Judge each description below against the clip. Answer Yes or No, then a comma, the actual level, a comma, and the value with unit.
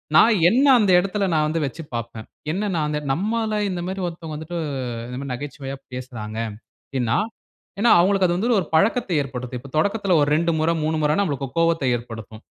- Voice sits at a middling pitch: Yes, medium, 160 Hz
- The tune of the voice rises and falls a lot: Yes, wide, 6.3 semitones